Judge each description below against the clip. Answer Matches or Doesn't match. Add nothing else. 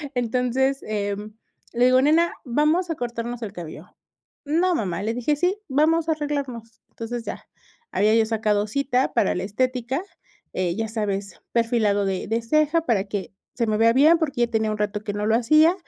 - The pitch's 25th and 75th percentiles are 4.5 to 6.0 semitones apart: Matches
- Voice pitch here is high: Matches